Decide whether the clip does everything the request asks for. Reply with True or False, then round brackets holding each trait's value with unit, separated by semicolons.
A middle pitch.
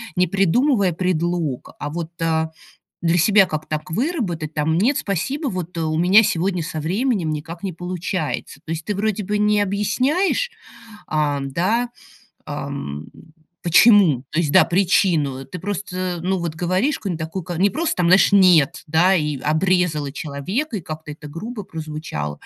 True (175 Hz)